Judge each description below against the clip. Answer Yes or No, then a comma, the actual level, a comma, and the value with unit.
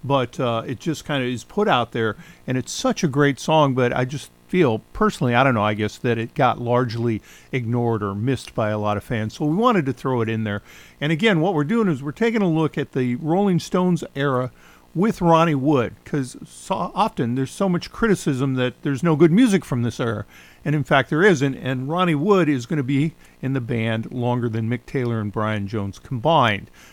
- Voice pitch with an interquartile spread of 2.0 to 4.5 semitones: No, average, 5.3 semitones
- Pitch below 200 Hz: Yes, low, 135 Hz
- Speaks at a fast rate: Yes, fast, 225 wpm